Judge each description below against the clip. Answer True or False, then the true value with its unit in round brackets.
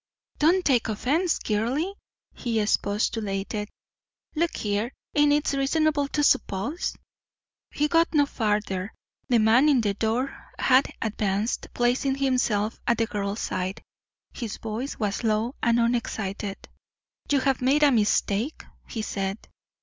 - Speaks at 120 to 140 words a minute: True (135 wpm)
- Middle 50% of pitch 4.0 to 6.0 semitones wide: True (5.0 semitones)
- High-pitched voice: True (235 Hz)